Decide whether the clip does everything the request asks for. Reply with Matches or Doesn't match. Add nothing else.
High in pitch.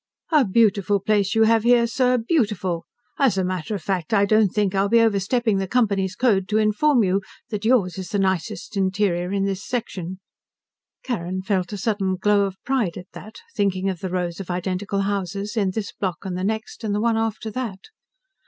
Matches